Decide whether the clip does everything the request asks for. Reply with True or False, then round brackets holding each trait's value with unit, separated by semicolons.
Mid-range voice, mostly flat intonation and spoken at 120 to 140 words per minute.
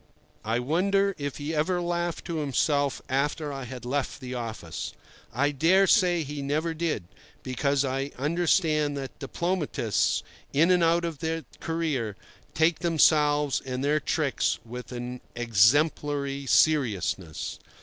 False (145 Hz; 4.0 semitones; 135 wpm)